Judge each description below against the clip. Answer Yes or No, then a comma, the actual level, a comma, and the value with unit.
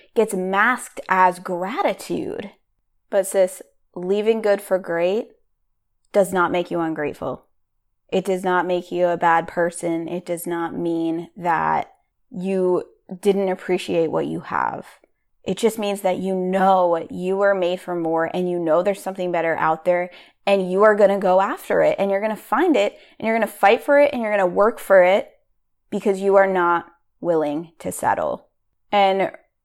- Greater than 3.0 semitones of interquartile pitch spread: No, narrow, 2.5 semitones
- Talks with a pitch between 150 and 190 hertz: Yes, medium, 185 Hz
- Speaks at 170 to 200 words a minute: Yes, average, 180 wpm